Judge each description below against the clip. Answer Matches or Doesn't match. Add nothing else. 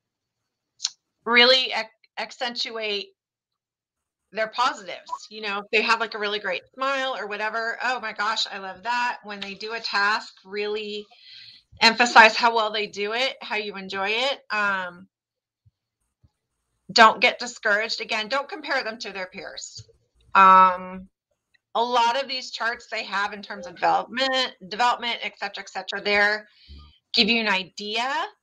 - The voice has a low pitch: Doesn't match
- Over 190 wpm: Doesn't match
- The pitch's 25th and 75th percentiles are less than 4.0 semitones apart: Matches